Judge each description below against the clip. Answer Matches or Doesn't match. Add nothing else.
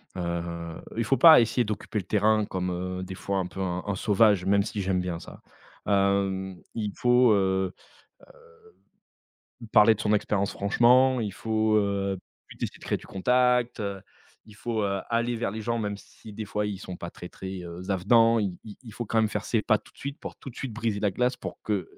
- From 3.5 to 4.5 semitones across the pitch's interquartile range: Doesn't match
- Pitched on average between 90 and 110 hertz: Matches